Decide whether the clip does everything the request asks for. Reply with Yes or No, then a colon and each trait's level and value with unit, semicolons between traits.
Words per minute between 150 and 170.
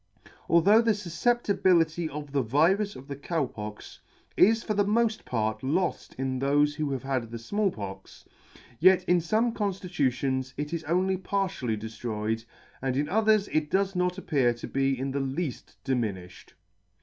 Yes: average, 160 wpm